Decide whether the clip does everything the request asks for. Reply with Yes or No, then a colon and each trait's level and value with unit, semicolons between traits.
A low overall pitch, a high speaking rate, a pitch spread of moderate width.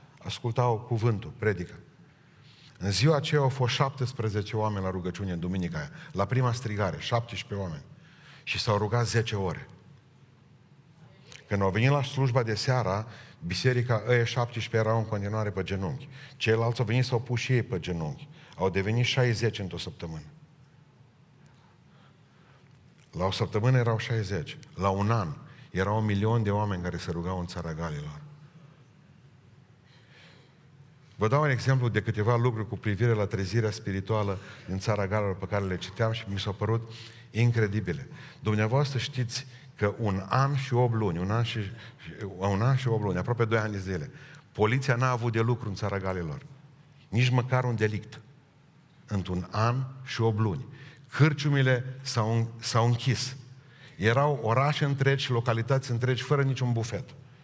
No: low, 120 Hz; average, 150 wpm; average, 4.4 semitones